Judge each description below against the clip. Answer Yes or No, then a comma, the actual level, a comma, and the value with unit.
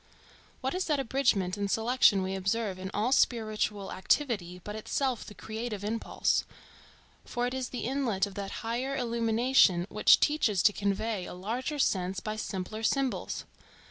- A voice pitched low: No, high, 220 Hz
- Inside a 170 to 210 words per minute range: No, average, 155 wpm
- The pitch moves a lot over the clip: No, average, 4.2 semitones